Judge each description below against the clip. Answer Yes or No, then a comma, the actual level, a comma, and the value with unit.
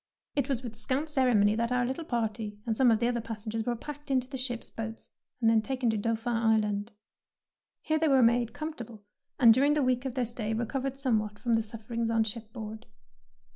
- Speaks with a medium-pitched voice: No, high, 235 Hz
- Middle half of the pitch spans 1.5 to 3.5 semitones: Yes, average, 2.7 semitones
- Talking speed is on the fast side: Yes, fast, 215 wpm